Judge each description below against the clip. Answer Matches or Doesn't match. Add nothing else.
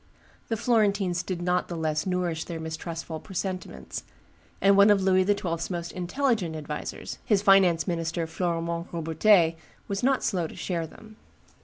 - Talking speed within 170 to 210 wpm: Doesn't match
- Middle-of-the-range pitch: Matches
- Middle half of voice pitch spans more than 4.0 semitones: Doesn't match